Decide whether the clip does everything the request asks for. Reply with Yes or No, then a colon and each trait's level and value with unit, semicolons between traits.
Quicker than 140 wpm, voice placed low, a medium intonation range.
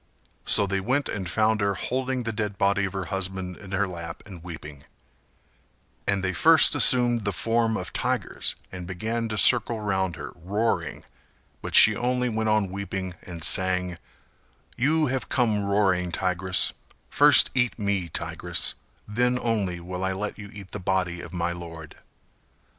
Yes: average, 165 wpm; low, 100 Hz; average, 3.5 semitones